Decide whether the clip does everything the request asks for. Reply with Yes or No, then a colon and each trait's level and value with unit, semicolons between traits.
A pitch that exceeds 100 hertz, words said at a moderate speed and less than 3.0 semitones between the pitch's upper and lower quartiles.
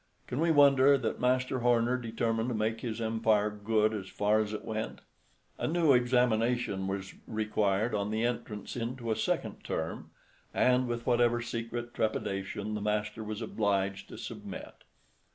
Yes: low, 115 Hz; average, 155 wpm; narrow, 2.5 semitones